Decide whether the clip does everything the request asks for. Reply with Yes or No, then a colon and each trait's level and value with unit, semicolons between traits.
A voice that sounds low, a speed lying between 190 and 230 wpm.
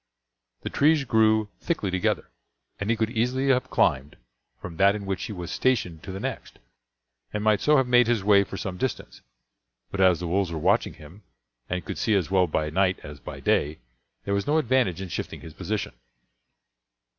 Yes: low, 100 Hz; average, 195 wpm